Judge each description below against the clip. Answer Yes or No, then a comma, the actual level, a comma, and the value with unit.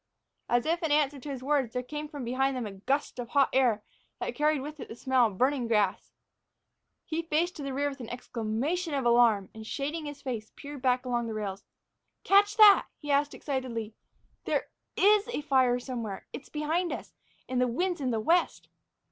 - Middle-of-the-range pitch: No, very high, 265 Hz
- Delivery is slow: No, average, 200 wpm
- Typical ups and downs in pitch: Yes, average, 3.9 semitones